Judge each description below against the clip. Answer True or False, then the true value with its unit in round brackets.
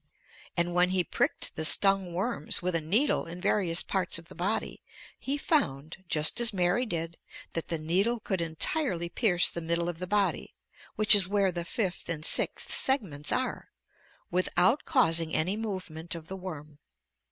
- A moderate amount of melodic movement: True (3.5 semitones)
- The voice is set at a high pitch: False (180 Hz)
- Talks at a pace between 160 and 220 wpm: True (170 wpm)